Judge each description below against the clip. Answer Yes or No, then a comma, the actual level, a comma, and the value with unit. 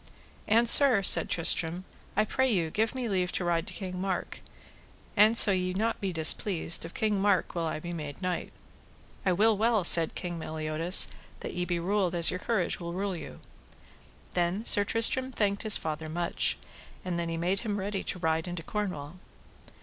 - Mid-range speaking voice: Yes, medium, 180 Hz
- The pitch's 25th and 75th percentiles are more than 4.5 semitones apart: No, average, 3.4 semitones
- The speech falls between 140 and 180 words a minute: No, average, 190 wpm